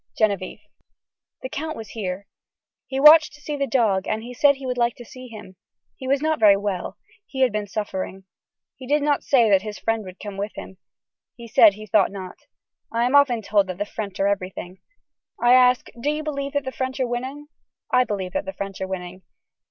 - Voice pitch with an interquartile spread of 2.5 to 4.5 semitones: No, average, 5.1 semitones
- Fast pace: Yes, fast, 215 wpm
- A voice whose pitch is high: Yes, high, 230 Hz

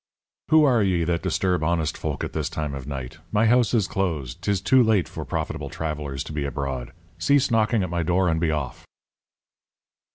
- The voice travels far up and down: Yes, wide, 5.8 semitones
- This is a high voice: No, very low, 85 Hz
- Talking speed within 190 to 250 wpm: Yes, average, 195 wpm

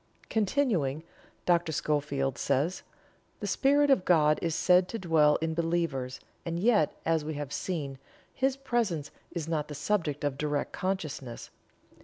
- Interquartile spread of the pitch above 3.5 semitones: Yes, average, 4.1 semitones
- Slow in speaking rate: No, average, 145 wpm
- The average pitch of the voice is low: No, medium, 165 Hz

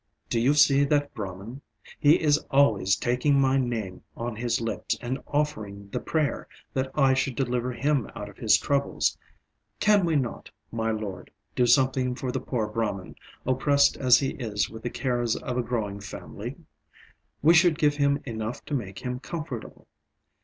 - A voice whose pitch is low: Yes, low, 125 Hz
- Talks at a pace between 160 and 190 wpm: Yes, average, 170 wpm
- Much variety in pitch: No, average, 4.0 semitones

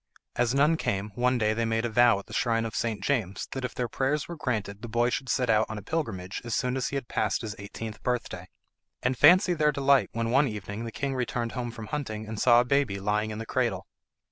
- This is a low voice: Yes, low, 120 Hz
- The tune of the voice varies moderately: Yes, average, 3.3 semitones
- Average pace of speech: No, fast, 245 wpm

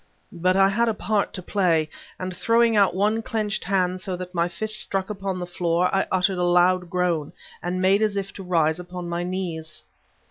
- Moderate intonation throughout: No, narrow, 2.0 semitones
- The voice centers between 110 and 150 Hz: No, medium, 185 Hz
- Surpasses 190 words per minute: Yes, fast, 205 wpm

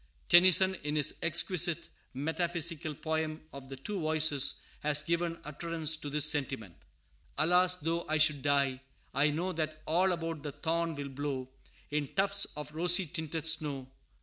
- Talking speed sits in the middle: Yes, average, 150 wpm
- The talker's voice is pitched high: No, medium, 155 Hz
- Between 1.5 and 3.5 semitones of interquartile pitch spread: Yes, average, 2.7 semitones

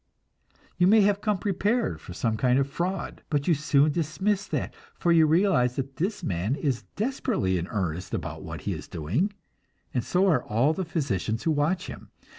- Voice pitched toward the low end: No, medium, 155 Hz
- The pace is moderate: Yes, average, 190 wpm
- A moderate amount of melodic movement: No, wide, 7.9 semitones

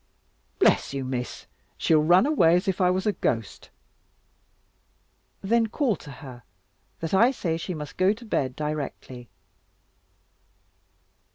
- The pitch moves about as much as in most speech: No, wide, 6.3 semitones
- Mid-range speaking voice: Yes, medium, 165 Hz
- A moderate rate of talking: No, slow, 130 wpm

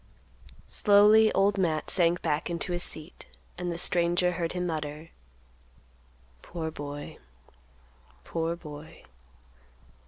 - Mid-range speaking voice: Yes, medium, 170 Hz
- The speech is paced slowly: Yes, slow, 105 wpm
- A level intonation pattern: Yes, narrow, 2.1 semitones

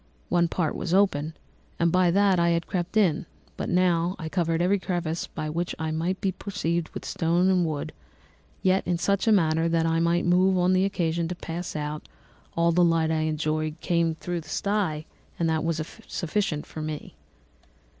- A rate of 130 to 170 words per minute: No, average, 190 wpm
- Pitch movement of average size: No, narrow, 2.3 semitones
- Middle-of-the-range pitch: Yes, medium, 170 Hz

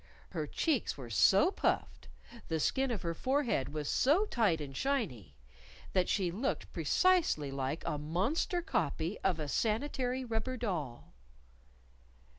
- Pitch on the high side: Yes, high, 195 Hz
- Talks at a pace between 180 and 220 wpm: No, slow, 135 wpm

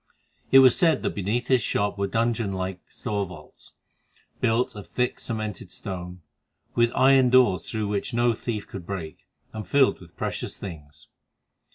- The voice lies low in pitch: Yes, low, 105 Hz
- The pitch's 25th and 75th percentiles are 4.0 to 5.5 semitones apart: Yes, average, 4.3 semitones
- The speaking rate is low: No, average, 160 wpm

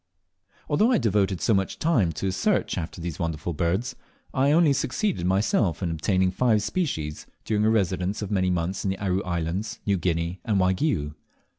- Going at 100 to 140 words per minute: No, average, 180 wpm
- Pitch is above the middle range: No, very low, 95 Hz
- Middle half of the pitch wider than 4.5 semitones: No, average, 4.2 semitones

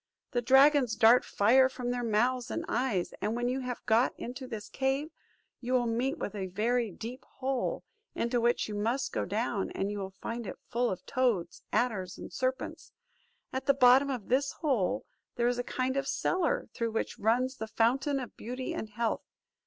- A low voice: No, high, 245 Hz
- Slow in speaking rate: No, average, 190 wpm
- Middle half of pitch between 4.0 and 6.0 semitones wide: No, average, 2.7 semitones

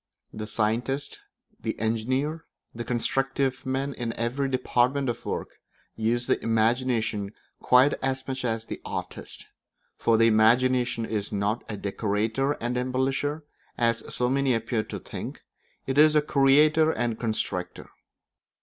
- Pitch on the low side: Yes, low, 125 Hz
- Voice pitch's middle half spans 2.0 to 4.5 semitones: Yes, average, 3.1 semitones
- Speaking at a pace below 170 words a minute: Yes, slow, 135 wpm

